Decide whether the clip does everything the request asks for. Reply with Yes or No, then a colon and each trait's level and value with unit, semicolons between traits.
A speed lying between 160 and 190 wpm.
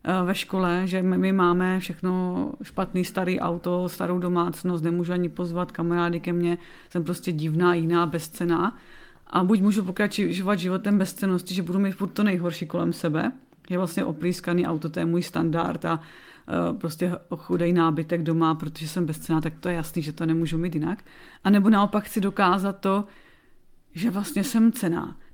Yes: fast, 170 wpm